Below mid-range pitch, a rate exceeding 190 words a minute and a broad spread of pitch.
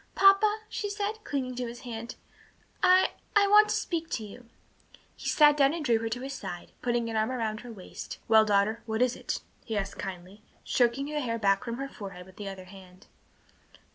No: high, 235 Hz; fast, 205 wpm; wide, 6.1 semitones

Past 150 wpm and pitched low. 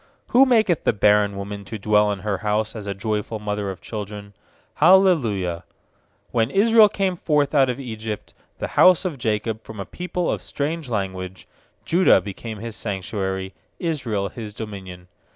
Yes: average, 160 wpm; low, 110 Hz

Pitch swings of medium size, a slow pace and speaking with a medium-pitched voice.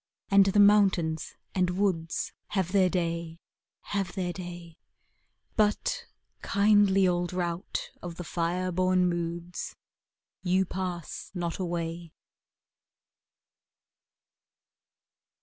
No: narrow, 1.9 semitones; slow, 95 wpm; medium, 180 Hz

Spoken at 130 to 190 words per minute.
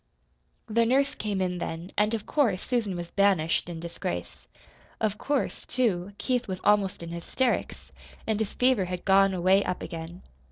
Yes: average, 165 wpm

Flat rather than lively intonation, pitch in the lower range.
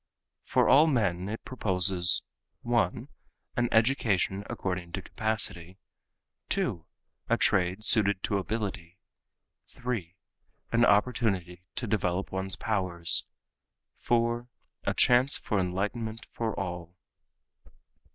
No: average, 4.0 semitones; low, 100 Hz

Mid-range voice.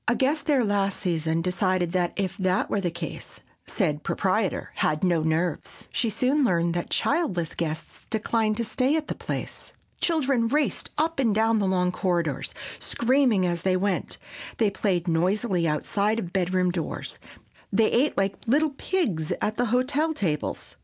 No: high, 195 Hz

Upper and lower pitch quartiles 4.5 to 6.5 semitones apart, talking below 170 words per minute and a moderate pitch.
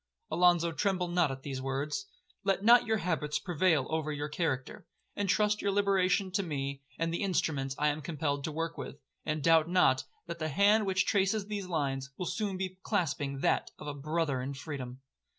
No: average, 4.8 semitones; average, 185 wpm; medium, 165 Hz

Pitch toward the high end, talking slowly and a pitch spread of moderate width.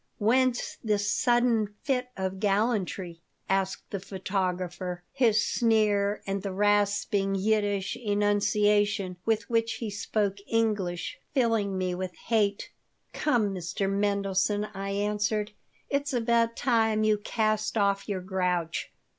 No: high, 205 Hz; slow, 120 wpm; narrow, 2.2 semitones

